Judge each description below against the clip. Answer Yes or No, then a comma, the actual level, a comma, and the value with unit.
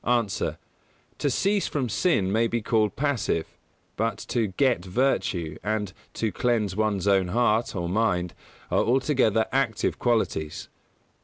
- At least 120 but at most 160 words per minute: Yes, average, 140 wpm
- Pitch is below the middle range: Yes, low, 110 Hz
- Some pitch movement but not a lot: Yes, average, 4.1 semitones